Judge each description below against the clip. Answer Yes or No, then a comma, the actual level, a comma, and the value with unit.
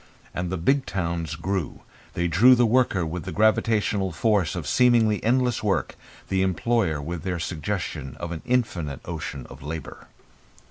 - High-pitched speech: No, very low, 95 Hz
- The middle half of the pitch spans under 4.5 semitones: No, average, 5.1 semitones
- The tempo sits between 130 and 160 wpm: Yes, average, 155 wpm